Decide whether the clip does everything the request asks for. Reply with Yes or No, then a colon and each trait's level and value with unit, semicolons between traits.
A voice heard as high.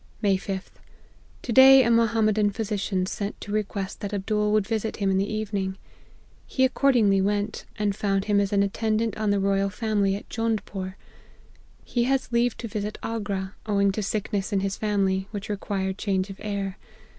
Yes: high, 205 Hz